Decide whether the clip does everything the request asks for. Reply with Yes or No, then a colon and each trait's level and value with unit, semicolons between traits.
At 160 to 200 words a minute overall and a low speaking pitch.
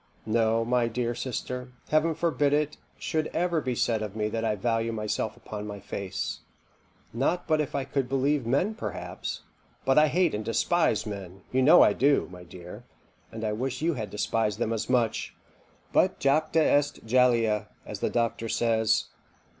Yes: average, 175 wpm; low, 120 Hz